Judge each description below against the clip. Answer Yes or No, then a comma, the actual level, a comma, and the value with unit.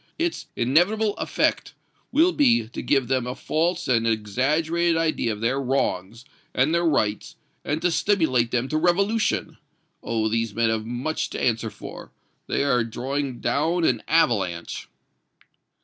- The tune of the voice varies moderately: No, wide, 6.5 semitones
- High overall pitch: No, low, 135 Hz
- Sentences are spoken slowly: No, average, 150 wpm